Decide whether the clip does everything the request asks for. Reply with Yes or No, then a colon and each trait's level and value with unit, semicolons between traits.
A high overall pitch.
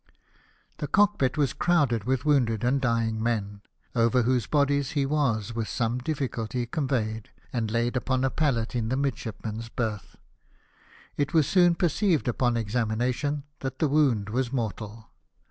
No: low, 125 Hz